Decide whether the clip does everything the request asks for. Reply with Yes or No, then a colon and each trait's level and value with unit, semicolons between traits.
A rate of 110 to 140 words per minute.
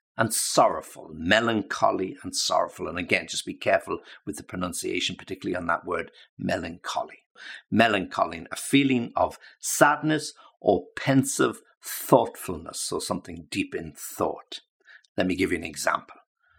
Yes: slow, 135 wpm